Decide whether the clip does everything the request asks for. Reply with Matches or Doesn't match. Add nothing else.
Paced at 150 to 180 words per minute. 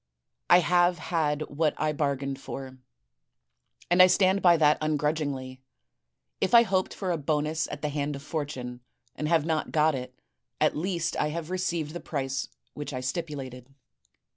Matches